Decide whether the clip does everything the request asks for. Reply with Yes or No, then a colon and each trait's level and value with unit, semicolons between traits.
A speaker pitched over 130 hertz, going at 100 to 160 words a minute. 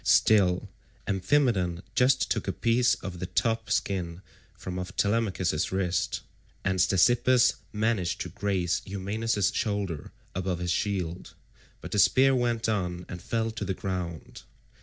No: very low, 95 Hz; average, 140 wpm